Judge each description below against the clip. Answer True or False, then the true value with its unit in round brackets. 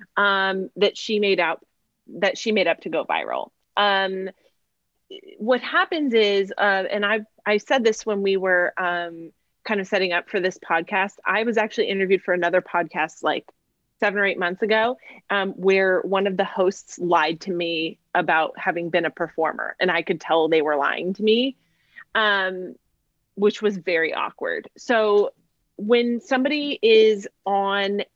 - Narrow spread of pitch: False (3.4 semitones)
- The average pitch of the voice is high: True (195 Hz)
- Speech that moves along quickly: False (170 wpm)